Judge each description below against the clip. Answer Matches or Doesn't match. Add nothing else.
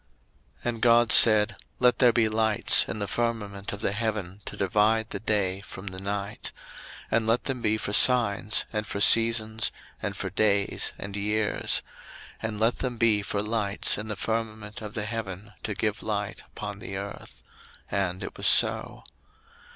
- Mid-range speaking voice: Doesn't match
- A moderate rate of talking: Matches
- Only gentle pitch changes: Matches